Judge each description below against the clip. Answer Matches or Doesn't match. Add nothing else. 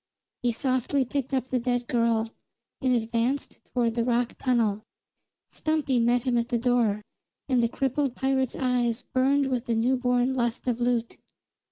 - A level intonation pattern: Matches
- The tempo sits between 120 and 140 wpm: Doesn't match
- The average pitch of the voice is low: Doesn't match